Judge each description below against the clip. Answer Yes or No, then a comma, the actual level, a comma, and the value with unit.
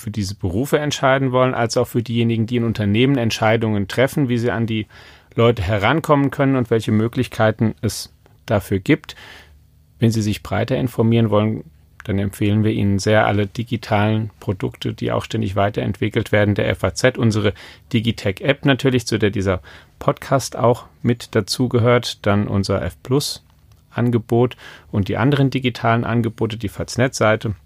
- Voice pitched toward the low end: Yes, low, 110 Hz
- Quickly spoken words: No, average, 150 wpm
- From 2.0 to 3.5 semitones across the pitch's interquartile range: Yes, average, 3.0 semitones